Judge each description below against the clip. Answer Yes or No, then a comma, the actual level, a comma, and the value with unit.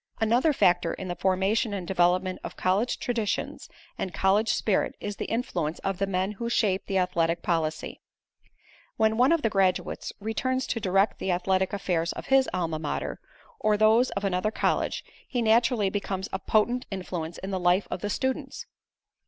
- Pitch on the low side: No, high, 195 Hz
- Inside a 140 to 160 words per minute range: No, average, 175 wpm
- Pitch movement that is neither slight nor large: Yes, average, 3.4 semitones